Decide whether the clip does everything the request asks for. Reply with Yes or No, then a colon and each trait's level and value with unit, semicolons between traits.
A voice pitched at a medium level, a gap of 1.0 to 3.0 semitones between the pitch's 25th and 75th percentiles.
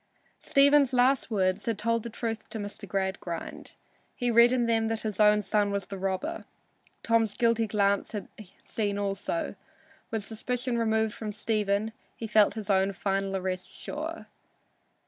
No: high, 215 Hz; narrow, 2.5 semitones